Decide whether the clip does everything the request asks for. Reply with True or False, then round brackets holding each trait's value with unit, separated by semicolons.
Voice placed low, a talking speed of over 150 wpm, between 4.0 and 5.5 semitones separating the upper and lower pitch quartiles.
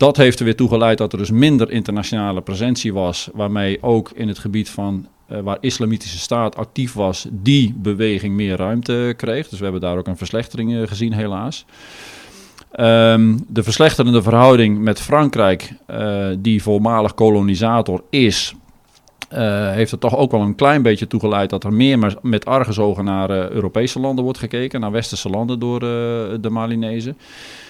False (110 Hz; 175 wpm; 2.7 semitones)